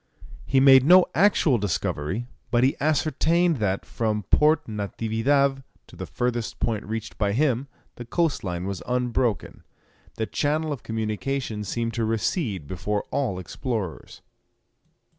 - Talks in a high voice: No, low, 120 Hz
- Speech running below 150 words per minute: Yes, slow, 135 wpm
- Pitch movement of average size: Yes, average, 4.9 semitones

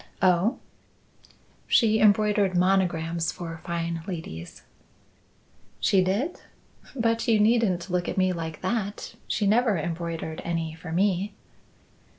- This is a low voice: No, medium, 185 Hz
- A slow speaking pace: Yes, slow, 115 wpm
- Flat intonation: No, average, 3.8 semitones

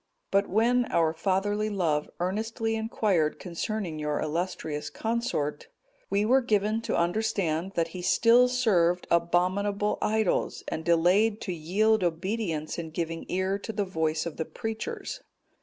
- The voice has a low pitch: No, high, 190 Hz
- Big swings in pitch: No, average, 4.7 semitones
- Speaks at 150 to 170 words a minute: No, average, 140 wpm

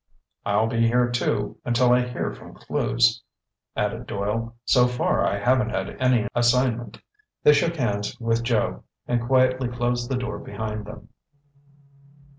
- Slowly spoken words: No, average, 145 wpm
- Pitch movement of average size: No, narrow, 2.0 semitones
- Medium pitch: No, low, 120 Hz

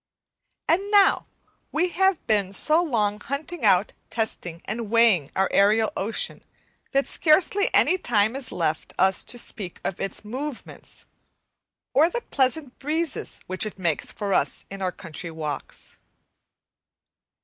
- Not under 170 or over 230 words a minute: No, average, 140 wpm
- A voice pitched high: Yes, high, 225 Hz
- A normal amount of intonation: No, wide, 8.0 semitones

